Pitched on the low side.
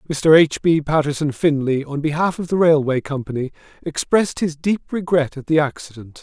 No: medium, 150 Hz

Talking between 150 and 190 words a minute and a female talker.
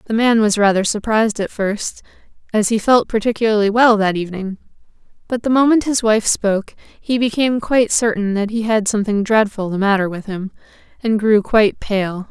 Yes: average, 180 wpm; female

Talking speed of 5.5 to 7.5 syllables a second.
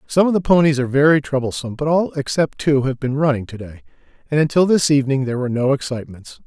Yes: 7.0 syllables/s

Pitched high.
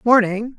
Yes: high, 225 Hz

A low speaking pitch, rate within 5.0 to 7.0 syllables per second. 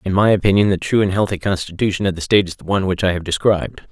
No: very low, 95 Hz; 7.5 syllables/s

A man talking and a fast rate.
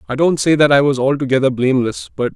Yes: male; fast, 230 wpm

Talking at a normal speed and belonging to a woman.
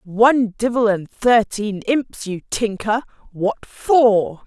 No: slow, 120 wpm; female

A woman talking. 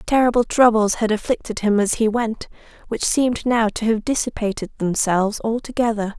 Yes: female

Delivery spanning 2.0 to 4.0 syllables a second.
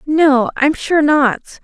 Yes: 3.2 syllables/s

